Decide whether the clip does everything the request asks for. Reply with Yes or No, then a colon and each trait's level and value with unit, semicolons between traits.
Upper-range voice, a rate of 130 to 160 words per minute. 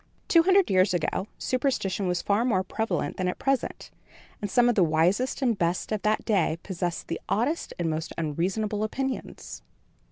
No: high, 200 Hz; average, 170 wpm